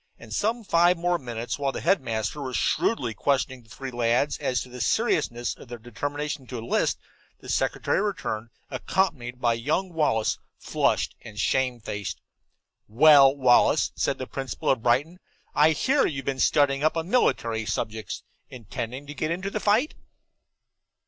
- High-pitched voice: No, low, 135 Hz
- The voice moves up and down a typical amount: Yes, average, 5.0 semitones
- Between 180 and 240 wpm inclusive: No, average, 155 wpm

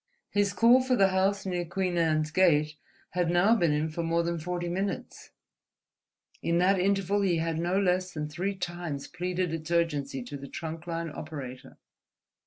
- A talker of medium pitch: Yes, medium, 175 Hz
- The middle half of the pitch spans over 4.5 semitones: No, average, 3.0 semitones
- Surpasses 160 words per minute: Yes, average, 175 wpm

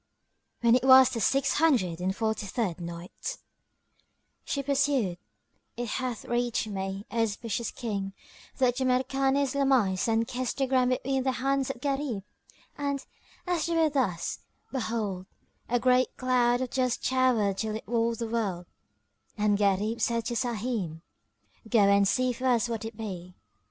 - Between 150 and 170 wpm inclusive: Yes, average, 155 wpm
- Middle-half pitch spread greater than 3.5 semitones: Yes, average, 3.9 semitones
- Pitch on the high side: Yes, high, 235 Hz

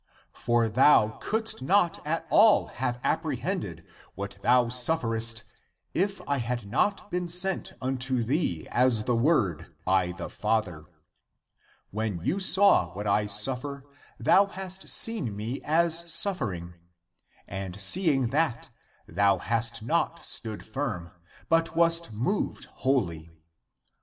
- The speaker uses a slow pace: Yes, slow, 125 wpm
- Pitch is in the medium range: No, low, 125 Hz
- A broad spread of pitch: Yes, wide, 7.9 semitones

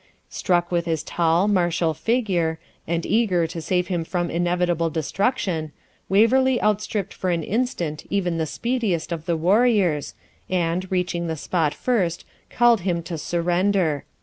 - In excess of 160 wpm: No, average, 150 wpm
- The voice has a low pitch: No, medium, 175 Hz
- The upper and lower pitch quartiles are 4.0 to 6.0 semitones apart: No, average, 3.3 semitones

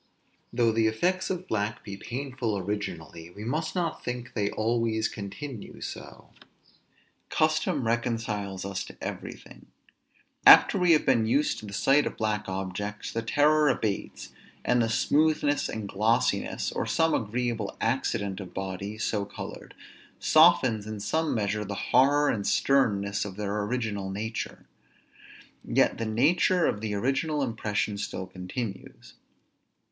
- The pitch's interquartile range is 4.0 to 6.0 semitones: Yes, average, 4.7 semitones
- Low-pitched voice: Yes, low, 110 Hz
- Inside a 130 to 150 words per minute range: Yes, average, 140 wpm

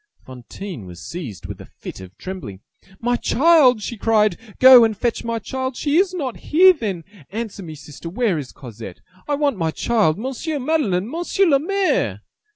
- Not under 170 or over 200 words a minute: Yes, average, 180 wpm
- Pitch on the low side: No, high, 225 Hz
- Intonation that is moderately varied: No, wide, 8.7 semitones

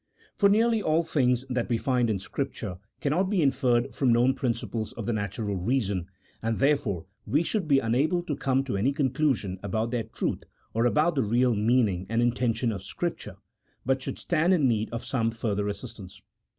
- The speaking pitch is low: Yes, low, 125 Hz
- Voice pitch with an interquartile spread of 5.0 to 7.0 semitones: No, average, 4.3 semitones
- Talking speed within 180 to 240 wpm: Yes, average, 185 wpm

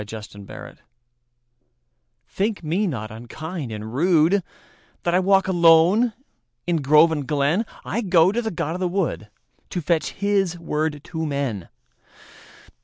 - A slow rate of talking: Yes, slow, 125 wpm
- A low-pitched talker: No, medium, 165 Hz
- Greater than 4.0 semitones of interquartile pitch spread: Yes, average, 4.7 semitones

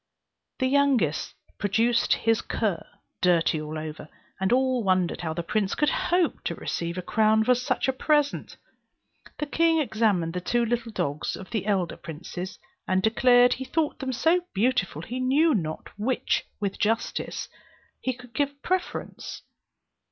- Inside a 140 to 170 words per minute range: Yes, average, 165 wpm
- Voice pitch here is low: No, high, 225 Hz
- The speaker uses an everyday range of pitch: No, wide, 6.2 semitones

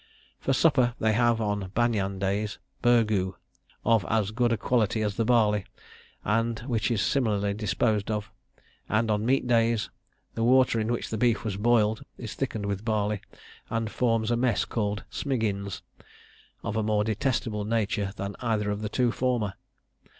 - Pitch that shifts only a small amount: Yes, narrow, 2.2 semitones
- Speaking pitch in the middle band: No, low, 110 Hz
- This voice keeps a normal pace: Yes, average, 165 wpm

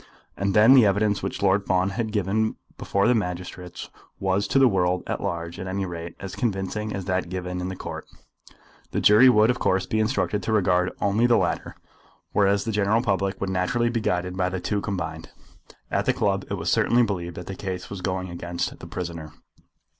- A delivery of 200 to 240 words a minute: Yes, fast, 205 wpm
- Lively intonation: No, average, 2.8 semitones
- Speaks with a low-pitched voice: Yes, very low, 95 Hz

